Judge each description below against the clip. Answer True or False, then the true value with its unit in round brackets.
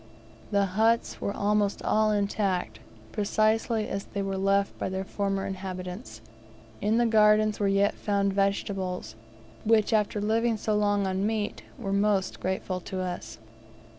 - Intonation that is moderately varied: False (1.8 semitones)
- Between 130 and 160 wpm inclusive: True (145 wpm)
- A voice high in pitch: True (200 Hz)